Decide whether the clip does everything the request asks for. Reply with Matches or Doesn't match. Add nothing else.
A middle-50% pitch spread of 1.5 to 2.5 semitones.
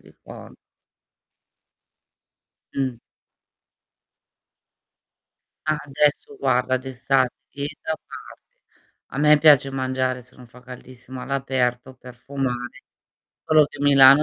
Matches